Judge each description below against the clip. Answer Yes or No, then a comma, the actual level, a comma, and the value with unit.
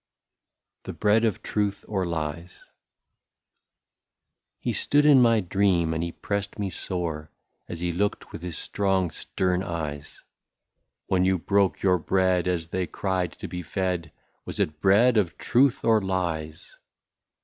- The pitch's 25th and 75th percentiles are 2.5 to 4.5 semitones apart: Yes, average, 3.1 semitones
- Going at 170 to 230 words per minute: No, average, 155 wpm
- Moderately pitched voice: No, very low, 95 Hz